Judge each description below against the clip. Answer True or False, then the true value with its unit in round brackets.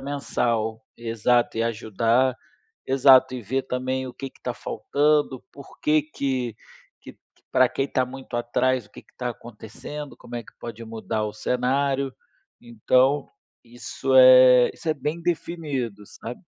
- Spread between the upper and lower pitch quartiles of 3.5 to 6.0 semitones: False (2.4 semitones)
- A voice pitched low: True (125 Hz)